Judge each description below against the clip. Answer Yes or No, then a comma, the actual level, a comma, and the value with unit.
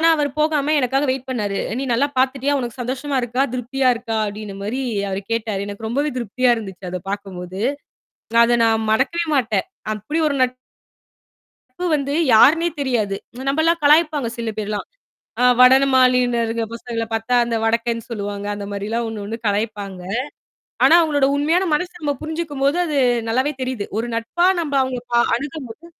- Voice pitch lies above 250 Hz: No, high, 245 Hz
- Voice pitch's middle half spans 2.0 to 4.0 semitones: No, average, 4.4 semitones